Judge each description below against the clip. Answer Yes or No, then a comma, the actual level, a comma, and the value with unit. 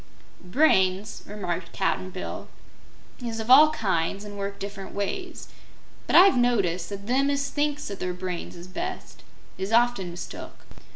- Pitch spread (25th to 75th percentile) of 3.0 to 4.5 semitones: No, average, 5.0 semitones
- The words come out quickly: No, average, 150 wpm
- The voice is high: Yes, high, 200 Hz